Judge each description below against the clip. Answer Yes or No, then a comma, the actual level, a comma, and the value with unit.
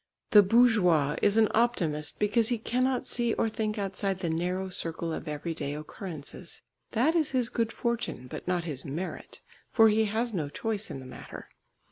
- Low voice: No, high, 200 Hz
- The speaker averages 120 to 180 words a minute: Yes, average, 175 wpm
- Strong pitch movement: Yes, wide, 5.7 semitones